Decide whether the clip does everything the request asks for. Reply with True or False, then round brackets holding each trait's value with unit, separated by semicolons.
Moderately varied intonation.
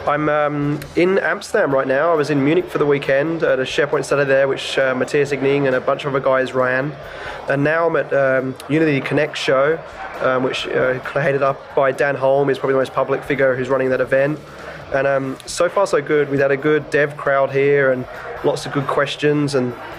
False (1.6 semitones)